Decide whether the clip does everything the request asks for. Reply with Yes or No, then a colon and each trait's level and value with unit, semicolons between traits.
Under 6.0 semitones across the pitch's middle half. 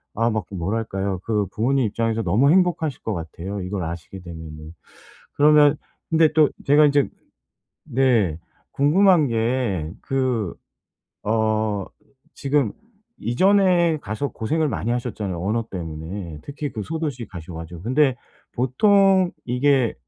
No: wide, 6.9 semitones